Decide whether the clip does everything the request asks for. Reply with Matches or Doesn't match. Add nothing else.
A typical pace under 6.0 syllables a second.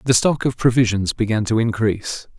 Matches